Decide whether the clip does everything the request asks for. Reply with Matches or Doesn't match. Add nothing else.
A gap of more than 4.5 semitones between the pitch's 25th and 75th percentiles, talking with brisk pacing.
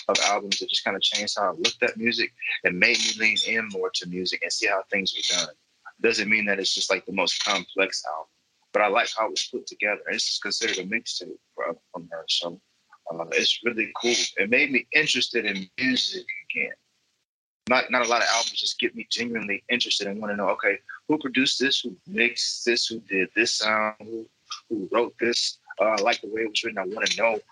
Matches